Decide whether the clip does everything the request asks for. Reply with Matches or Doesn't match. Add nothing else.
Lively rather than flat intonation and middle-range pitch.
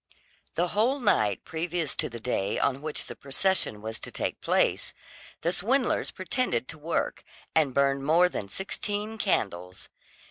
Matches